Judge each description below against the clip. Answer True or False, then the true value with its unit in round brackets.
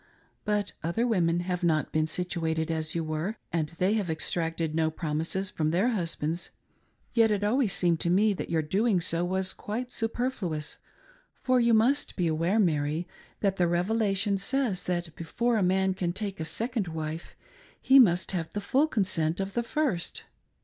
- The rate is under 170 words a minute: False (175 wpm)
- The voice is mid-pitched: True (180 Hz)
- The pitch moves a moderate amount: True (4.5 semitones)